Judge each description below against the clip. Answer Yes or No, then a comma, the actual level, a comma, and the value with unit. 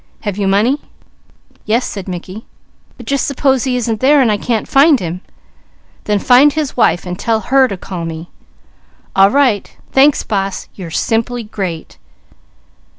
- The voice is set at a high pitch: Yes, high, 220 Hz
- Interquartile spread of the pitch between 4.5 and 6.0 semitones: Yes, wide, 5.4 semitones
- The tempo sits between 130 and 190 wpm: Yes, average, 155 wpm